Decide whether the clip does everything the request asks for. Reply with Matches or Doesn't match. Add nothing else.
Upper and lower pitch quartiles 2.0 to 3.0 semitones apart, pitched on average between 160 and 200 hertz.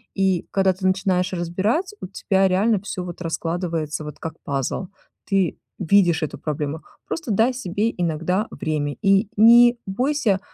Doesn't match